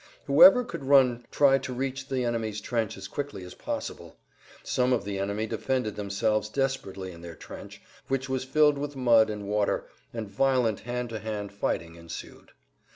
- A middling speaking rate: Yes, average, 170 wpm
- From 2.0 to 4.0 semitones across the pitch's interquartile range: No, average, 4.6 semitones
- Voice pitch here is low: Yes, low, 115 Hz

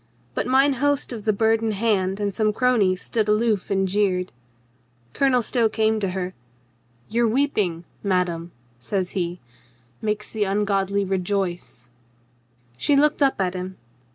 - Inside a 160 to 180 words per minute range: No, average, 150 wpm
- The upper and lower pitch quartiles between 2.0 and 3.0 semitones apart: No, average, 3.4 semitones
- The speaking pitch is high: Yes, high, 205 Hz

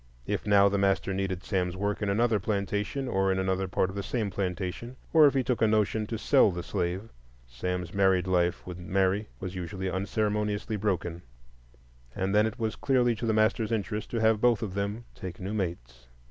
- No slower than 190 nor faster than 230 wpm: Yes, average, 200 wpm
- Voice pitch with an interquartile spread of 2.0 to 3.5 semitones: Yes, average, 2.7 semitones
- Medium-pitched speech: No, low, 100 Hz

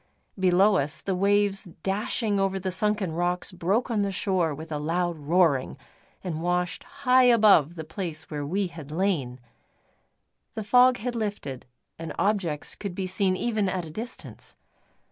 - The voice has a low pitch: No, medium, 185 Hz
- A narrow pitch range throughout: No, average, 4.0 semitones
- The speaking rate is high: No, average, 160 wpm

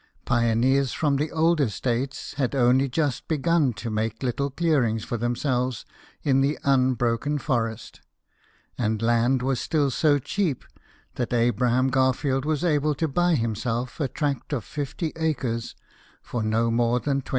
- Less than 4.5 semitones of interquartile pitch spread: Yes, average, 3.5 semitones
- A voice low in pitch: Yes, low, 130 Hz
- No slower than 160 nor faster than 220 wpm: No, average, 150 wpm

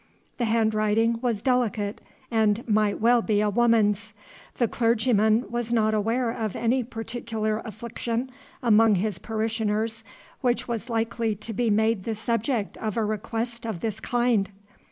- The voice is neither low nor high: No, high, 225 Hz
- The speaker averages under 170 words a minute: Yes, average, 145 wpm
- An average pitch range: No, narrow, 1.6 semitones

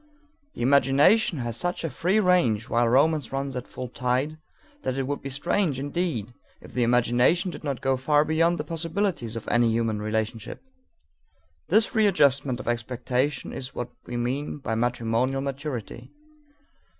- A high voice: No, low, 135 Hz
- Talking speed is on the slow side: No, average, 155 wpm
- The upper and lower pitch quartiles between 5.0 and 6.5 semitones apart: No, average, 4.2 semitones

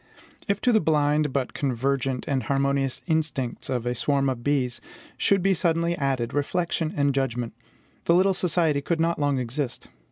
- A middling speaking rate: Yes, average, 165 wpm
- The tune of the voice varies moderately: Yes, average, 3.9 semitones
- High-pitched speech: No, medium, 140 Hz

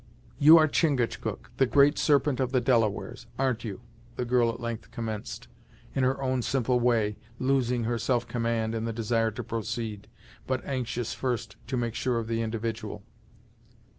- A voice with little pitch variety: Yes, narrow, 2.2 semitones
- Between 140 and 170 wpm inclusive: Yes, average, 165 wpm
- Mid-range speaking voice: No, low, 120 Hz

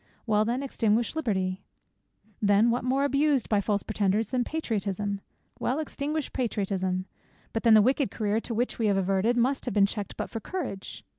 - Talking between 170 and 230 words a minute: Yes, average, 175 wpm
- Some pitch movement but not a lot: Yes, average, 4.0 semitones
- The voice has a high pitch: Yes, high, 220 Hz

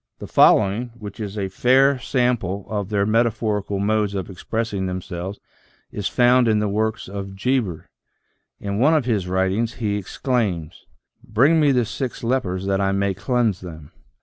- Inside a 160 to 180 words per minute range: Yes, average, 175 wpm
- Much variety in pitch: No, average, 3.8 semitones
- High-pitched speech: No, low, 105 Hz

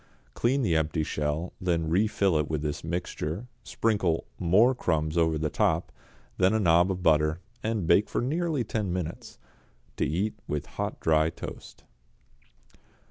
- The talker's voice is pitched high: No, very low, 85 Hz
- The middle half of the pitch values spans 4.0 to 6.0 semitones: Yes, average, 5.0 semitones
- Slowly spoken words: No, average, 150 wpm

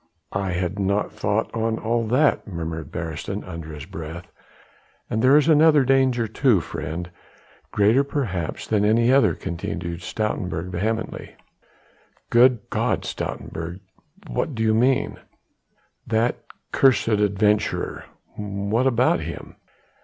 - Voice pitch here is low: Yes, low, 105 Hz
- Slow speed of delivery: Yes, slow, 130 wpm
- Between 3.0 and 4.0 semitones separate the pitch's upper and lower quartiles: No, average, 5.3 semitones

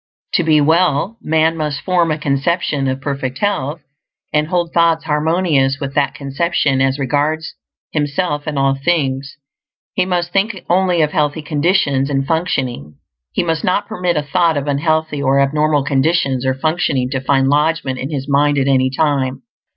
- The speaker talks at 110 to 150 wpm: No, average, 165 wpm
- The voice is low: No, medium, 150 Hz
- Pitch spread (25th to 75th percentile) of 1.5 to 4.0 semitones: Yes, average, 3.4 semitones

